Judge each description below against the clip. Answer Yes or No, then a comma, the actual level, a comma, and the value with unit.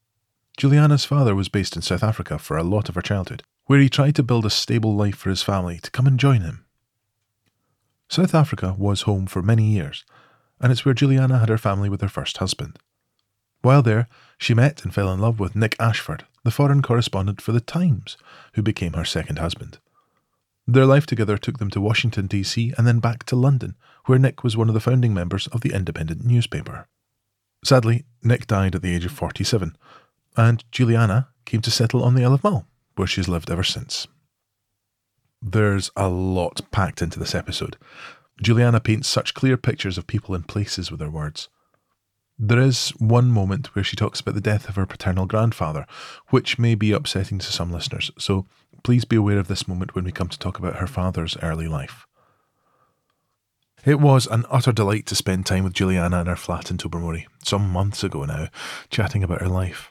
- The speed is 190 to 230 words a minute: Yes, average, 195 wpm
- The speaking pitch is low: Yes, low, 110 Hz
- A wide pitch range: No, average, 4.3 semitones